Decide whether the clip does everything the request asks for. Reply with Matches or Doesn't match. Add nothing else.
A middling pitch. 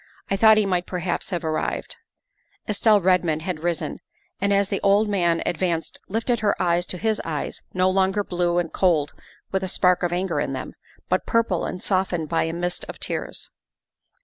Matches